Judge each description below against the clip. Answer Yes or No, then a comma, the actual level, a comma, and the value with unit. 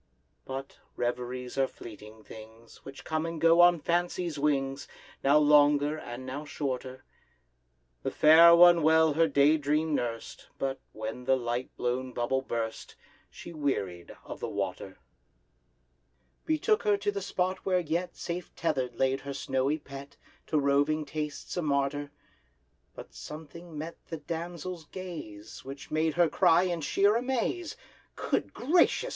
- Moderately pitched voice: Yes, medium, 145 Hz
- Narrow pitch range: No, average, 4.2 semitones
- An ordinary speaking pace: Yes, average, 145 wpm